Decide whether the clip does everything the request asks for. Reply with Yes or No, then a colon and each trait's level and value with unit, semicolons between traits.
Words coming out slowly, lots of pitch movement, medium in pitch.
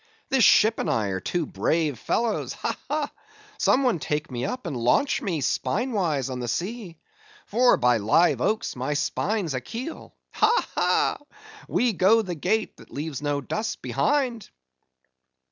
No: average, 155 wpm; wide, 8.9 semitones; medium, 180 Hz